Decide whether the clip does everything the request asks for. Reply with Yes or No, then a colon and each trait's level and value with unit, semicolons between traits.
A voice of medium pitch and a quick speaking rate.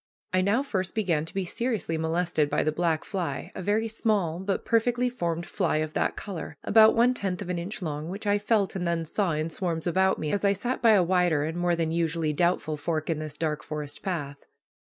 Yes: medium, 175 Hz; fast, 225 wpm